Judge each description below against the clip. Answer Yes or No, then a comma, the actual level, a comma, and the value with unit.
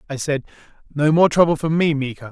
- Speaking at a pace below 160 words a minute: No, fast, 205 wpm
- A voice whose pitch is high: No, medium, 150 Hz